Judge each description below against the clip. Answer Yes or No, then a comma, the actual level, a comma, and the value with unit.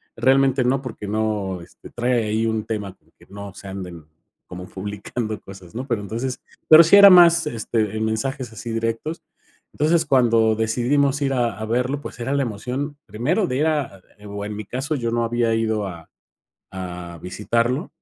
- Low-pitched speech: Yes, low, 115 Hz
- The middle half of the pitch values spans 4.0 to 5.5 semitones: Yes, average, 4.4 semitones